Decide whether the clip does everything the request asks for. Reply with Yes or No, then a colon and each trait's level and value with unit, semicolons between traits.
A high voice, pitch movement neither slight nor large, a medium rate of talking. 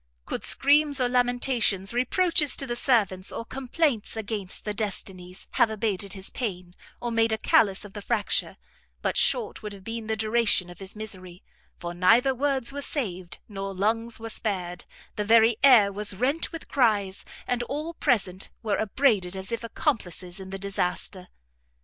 Yes: high, 220 Hz; average, 4.2 semitones; average, 170 wpm